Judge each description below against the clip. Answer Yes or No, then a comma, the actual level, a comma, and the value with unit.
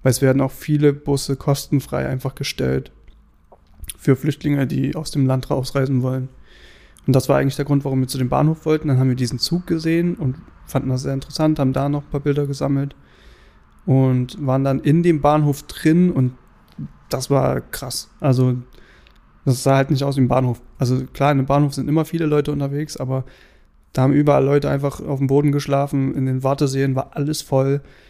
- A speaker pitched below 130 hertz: No, low, 135 Hz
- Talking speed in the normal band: No, fast, 200 wpm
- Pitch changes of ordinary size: No, narrow, 1.9 semitones